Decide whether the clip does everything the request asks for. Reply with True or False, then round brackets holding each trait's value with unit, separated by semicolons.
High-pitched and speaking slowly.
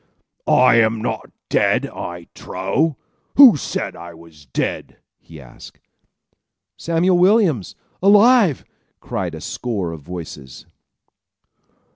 False (115 Hz; 105 wpm)